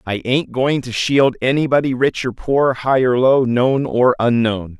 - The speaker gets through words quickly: No, average, 190 wpm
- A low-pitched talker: Yes, low, 125 Hz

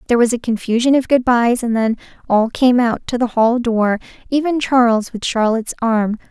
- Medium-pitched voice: No, high, 235 Hz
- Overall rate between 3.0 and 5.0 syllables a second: No, 5.2 syllables/s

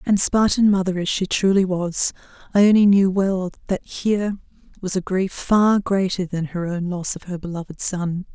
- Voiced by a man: No, female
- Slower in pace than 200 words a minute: Yes, average, 180 wpm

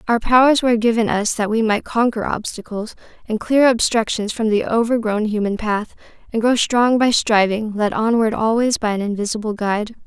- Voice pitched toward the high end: Yes, high, 220 Hz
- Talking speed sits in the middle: Yes, average, 180 wpm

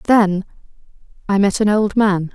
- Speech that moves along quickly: No, average, 155 wpm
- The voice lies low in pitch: No, high, 200 Hz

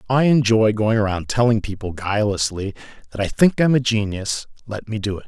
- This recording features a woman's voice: No, male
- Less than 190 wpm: No, fast, 205 wpm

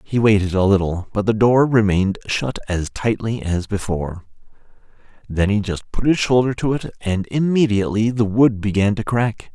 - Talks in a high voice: No, low, 105 Hz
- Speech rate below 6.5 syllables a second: Yes, 5.1 syllables/s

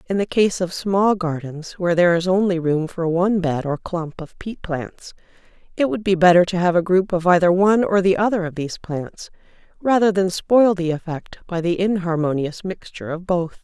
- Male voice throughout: No, female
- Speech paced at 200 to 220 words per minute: Yes, fast, 205 wpm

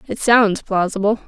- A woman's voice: Yes, female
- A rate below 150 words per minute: Yes, average, 140 wpm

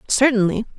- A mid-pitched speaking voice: No, high, 230 Hz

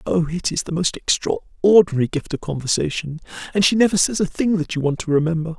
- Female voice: No, male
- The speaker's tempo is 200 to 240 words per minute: Yes, fast, 205 wpm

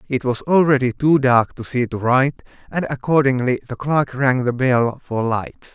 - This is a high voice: No, low, 130 Hz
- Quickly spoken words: No, average, 190 wpm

